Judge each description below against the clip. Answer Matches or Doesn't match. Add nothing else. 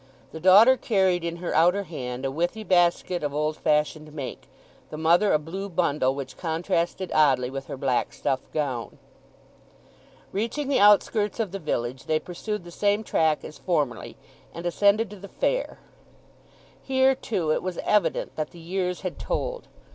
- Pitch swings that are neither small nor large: Matches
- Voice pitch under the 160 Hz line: Doesn't match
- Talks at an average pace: Matches